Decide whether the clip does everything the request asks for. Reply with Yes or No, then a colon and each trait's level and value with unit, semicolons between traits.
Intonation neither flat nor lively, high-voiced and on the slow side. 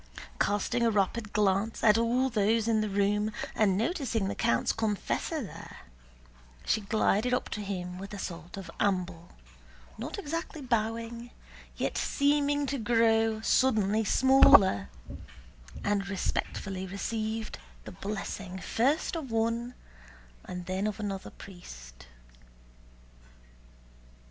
Yes: average, 3.1 semitones; high, 215 Hz; slow, 120 wpm